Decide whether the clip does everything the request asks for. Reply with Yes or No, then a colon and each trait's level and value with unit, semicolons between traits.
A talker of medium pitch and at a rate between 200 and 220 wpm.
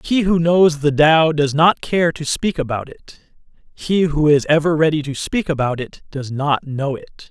Yes: medium, 155 Hz; fast, 205 wpm